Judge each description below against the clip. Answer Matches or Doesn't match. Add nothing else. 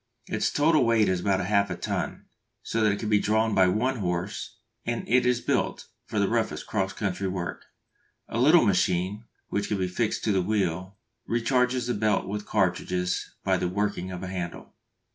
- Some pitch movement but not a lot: Matches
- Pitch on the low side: Matches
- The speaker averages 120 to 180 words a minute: Doesn't match